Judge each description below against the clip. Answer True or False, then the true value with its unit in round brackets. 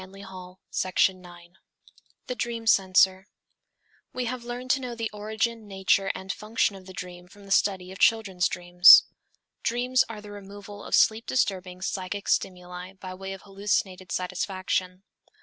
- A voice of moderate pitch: False (195 Hz)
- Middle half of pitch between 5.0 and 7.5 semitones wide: False (2.8 semitones)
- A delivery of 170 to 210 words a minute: False (155 wpm)